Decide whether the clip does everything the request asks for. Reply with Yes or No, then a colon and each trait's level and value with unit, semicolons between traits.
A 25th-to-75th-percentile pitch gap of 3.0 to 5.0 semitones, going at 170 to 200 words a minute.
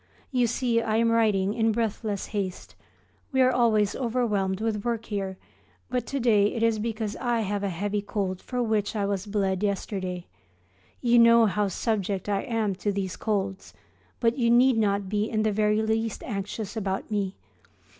No: narrow, 2.4 semitones; average, 175 wpm